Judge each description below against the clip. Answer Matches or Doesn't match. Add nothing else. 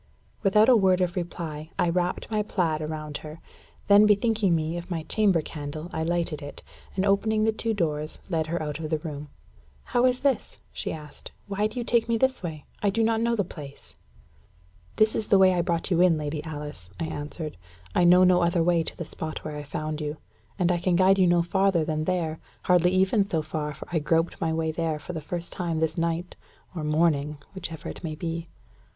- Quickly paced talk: Matches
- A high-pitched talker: Doesn't match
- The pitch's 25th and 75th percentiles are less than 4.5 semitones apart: Matches